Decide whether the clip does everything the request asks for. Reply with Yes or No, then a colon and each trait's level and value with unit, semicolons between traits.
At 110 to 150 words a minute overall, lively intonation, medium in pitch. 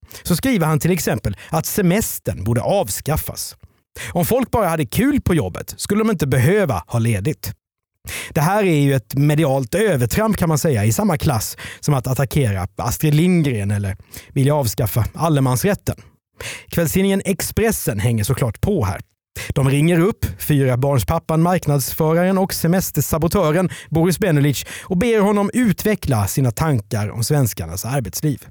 Yes: average, 145 wpm; wide, 6.3 semitones; medium, 145 Hz